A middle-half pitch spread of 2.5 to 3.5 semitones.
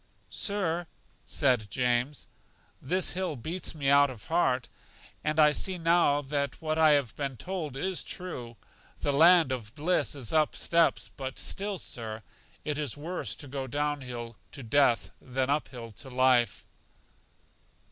No: average, 4.2 semitones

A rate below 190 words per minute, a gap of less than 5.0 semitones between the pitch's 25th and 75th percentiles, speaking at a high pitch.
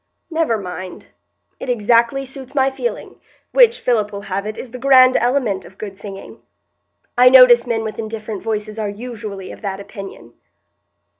Yes: average, 160 wpm; average, 3.9 semitones; high, 225 Hz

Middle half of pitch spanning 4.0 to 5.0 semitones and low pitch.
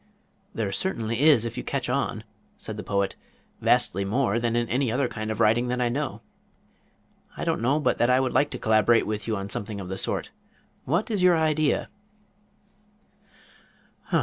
Yes: average, 4.3 semitones; low, 120 Hz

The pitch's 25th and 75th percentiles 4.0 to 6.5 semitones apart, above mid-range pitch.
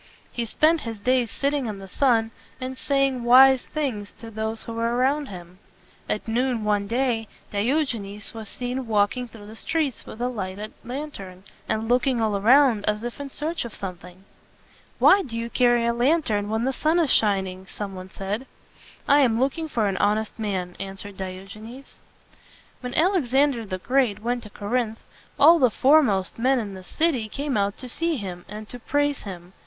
Yes: average, 4.5 semitones; high, 230 Hz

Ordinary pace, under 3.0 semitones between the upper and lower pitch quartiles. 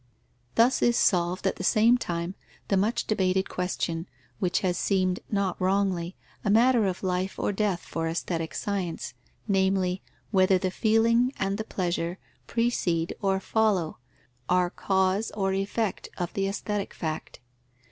Yes: average, 145 wpm; narrow, 2.4 semitones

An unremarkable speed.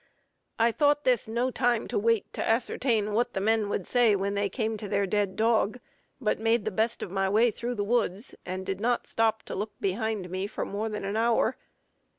No: fast, 215 wpm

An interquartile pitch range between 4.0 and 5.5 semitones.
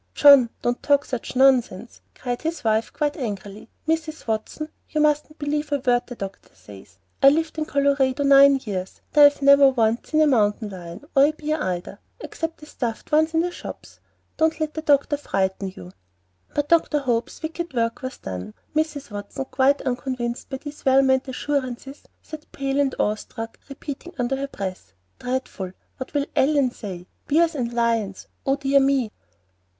Yes: average, 4.3 semitones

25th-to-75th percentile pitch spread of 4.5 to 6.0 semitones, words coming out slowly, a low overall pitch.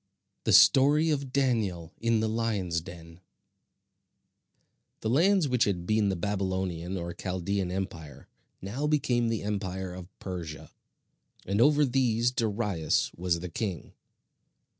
Yes: average, 5.1 semitones; slow, 125 wpm; low, 100 Hz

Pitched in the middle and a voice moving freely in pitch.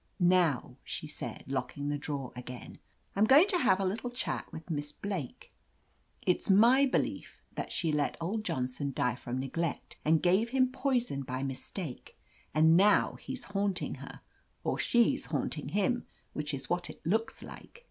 Yes: medium, 175 Hz; wide, 7.4 semitones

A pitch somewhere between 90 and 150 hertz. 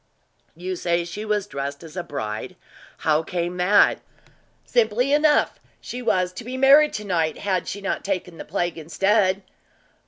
No: medium, 185 Hz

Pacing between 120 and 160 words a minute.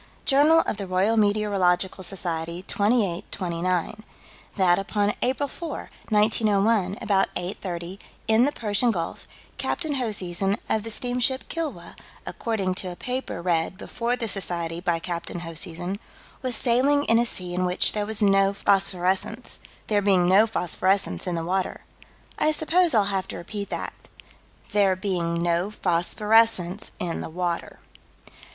Yes: average, 145 wpm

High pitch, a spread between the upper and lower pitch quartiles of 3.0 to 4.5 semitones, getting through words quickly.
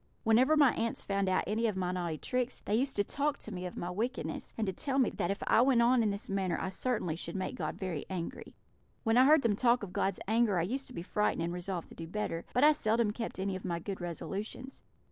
No: high, 210 Hz; average, 5.0 semitones; fast, 260 wpm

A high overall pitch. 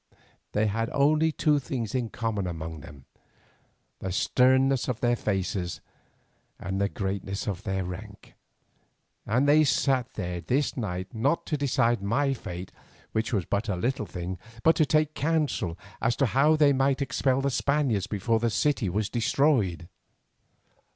No: low, 115 Hz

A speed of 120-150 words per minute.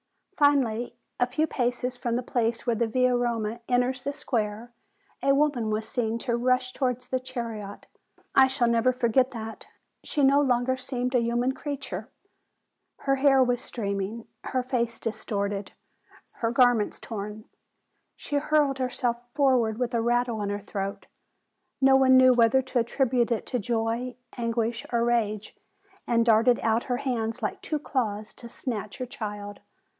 No: average, 165 wpm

